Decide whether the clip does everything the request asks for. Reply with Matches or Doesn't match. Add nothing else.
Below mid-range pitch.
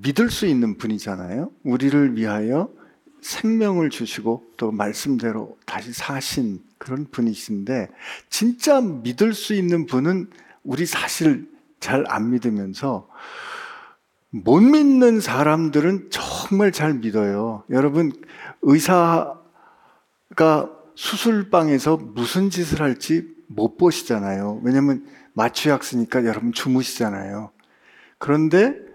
Doesn't match